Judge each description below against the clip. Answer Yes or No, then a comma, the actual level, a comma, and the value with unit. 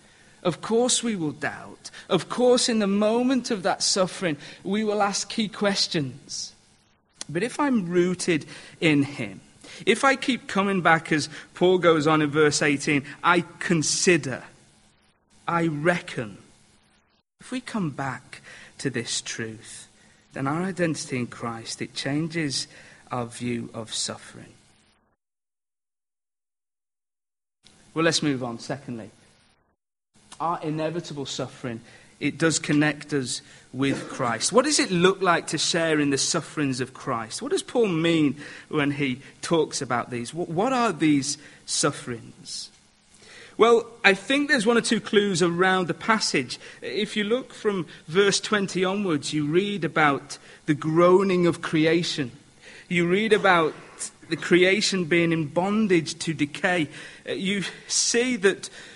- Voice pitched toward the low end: No, medium, 165 Hz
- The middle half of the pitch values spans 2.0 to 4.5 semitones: No, wide, 5.6 semitones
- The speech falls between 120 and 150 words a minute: Yes, slow, 135 wpm